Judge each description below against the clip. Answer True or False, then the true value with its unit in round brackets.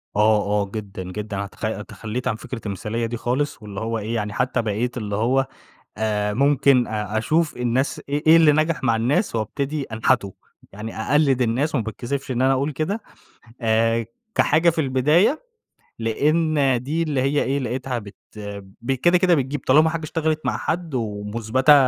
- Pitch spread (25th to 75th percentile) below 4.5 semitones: False (5.0 semitones)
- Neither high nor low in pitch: False (125 Hz)